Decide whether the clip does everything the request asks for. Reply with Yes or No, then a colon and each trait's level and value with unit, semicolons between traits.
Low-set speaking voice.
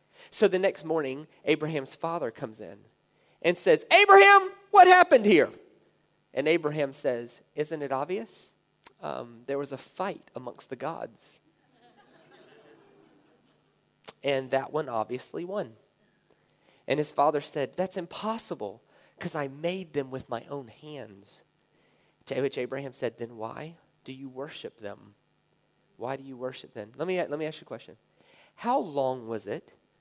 No: medium, 145 Hz